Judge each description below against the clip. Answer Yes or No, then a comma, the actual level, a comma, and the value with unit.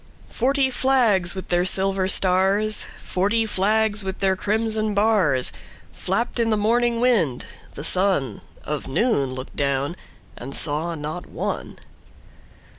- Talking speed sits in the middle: No, slow, 115 wpm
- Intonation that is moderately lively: Yes, average, 4.8 semitones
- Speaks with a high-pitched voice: Yes, high, 195 Hz